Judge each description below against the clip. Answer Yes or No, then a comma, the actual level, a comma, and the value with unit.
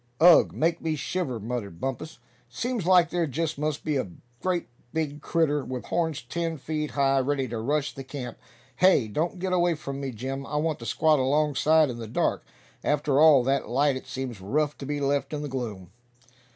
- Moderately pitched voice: Yes, medium, 145 Hz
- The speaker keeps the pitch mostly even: No, average, 3.4 semitones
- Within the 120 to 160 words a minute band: No, average, 195 wpm